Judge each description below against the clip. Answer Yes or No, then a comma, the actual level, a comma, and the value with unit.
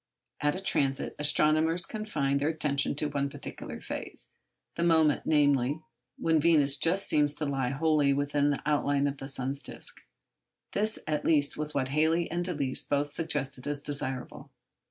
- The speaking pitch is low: No, medium, 145 Hz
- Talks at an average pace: Yes, average, 155 wpm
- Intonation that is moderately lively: No, narrow, 2.1 semitones